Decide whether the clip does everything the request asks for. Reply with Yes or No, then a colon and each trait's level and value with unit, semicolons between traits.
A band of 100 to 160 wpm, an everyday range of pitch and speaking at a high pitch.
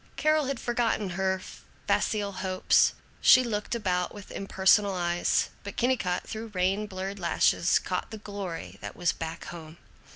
Yes: average, 150 wpm; average, 3.2 semitones; high, 195 Hz